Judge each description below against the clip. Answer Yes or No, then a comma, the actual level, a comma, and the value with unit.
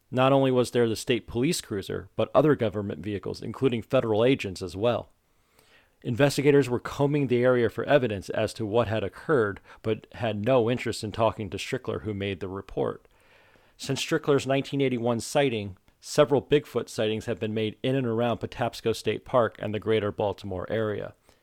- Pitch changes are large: No, average, 3.6 semitones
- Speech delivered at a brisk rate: No, average, 175 wpm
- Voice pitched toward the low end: Yes, low, 115 Hz